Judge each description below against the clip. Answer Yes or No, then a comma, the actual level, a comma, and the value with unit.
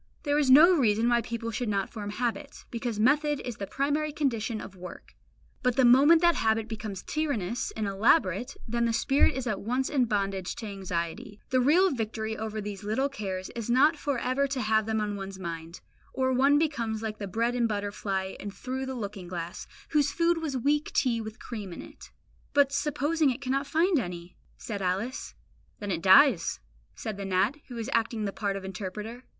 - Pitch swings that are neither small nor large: Yes, average, 4.9 semitones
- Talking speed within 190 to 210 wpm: Yes, average, 200 wpm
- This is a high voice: Yes, high, 230 Hz